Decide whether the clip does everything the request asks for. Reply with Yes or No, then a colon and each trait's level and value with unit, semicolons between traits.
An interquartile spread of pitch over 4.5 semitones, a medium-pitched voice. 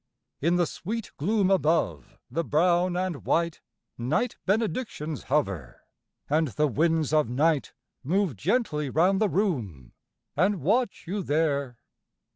Yes: average, 4.9 semitones; medium, 165 Hz